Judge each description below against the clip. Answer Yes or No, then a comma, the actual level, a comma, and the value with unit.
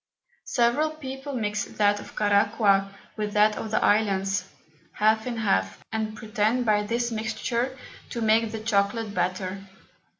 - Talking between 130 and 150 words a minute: Yes, average, 140 wpm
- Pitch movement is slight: Yes, narrow, 2.3 semitones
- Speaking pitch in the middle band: No, high, 215 Hz